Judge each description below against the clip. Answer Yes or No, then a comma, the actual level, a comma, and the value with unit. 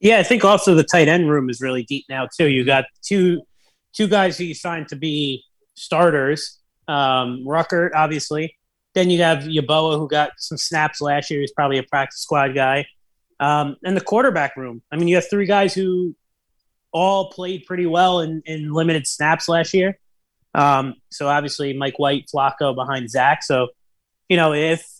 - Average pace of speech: Yes, average, 185 wpm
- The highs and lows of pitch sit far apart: No, average, 4.1 semitones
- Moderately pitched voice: Yes, medium, 155 Hz